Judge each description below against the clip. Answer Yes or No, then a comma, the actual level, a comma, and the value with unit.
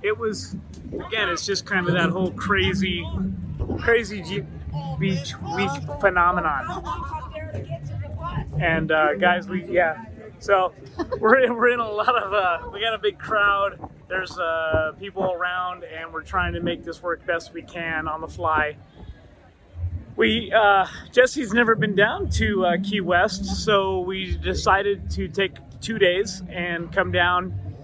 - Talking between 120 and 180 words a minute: Yes, average, 155 wpm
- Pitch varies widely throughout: No, average, 4.8 semitones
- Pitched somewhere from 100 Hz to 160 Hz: No, medium, 180 Hz